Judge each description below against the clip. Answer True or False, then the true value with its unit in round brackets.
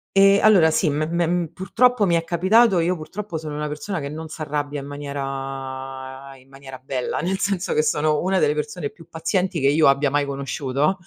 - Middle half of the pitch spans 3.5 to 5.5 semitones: True (4.3 semitones)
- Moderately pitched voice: True (155 Hz)